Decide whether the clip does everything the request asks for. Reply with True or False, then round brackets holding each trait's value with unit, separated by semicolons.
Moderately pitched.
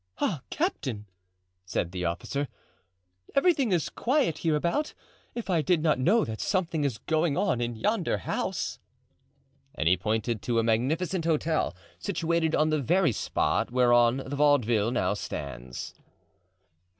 True (145 Hz)